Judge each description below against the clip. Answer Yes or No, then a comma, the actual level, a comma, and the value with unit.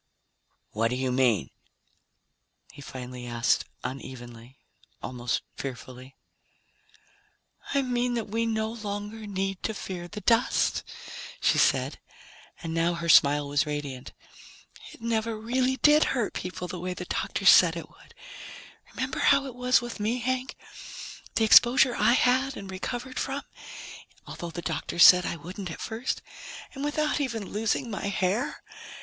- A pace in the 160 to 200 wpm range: No, average, 145 wpm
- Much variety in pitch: Yes, wide, 8.5 semitones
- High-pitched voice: Yes, high, 200 Hz